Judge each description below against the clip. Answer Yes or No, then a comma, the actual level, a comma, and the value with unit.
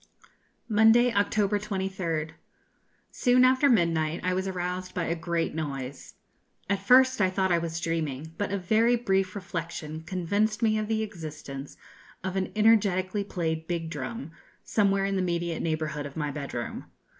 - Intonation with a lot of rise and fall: No, average, 4.3 semitones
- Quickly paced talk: No, average, 155 wpm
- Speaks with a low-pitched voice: No, medium, 185 Hz